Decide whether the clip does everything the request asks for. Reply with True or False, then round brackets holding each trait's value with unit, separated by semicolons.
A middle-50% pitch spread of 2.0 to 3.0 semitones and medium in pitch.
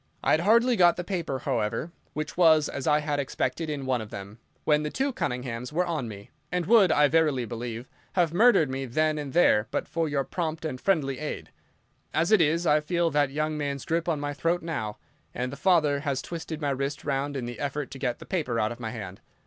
False (4.2 semitones; 150 Hz)